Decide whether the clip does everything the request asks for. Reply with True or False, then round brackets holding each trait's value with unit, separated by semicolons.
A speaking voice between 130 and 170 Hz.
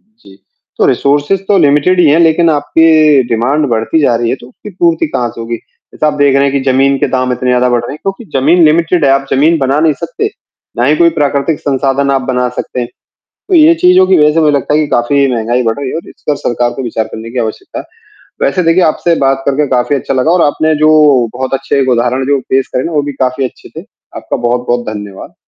True (140 Hz)